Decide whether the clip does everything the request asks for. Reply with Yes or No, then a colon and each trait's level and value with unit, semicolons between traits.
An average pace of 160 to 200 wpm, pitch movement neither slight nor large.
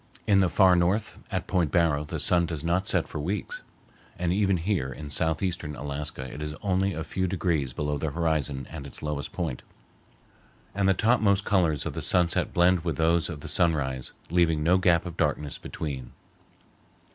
Yes: average, 180 wpm; average, 3.6 semitones